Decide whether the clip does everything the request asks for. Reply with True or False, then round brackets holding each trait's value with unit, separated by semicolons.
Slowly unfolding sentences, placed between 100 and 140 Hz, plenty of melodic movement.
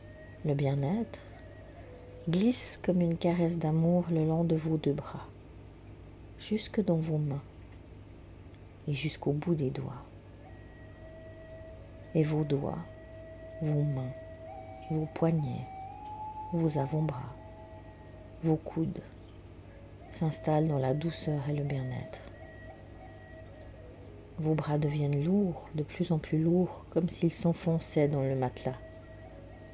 True (110 wpm; 135 Hz; 7.1 semitones)